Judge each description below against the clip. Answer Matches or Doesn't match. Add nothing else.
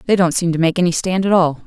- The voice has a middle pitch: Matches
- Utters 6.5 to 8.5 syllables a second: Matches